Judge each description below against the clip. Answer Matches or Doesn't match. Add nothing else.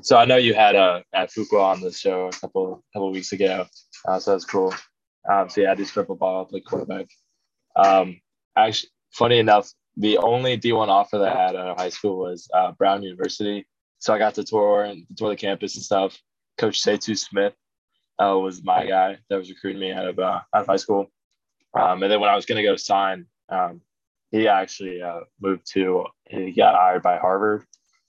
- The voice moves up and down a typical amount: Doesn't match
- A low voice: Matches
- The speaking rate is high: Matches